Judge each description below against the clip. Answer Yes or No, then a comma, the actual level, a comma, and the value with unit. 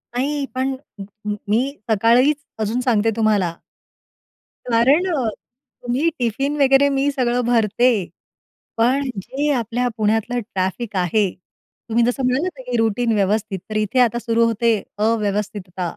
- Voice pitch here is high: Yes, high, 235 Hz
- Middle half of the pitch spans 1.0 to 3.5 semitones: Yes, average, 3.2 semitones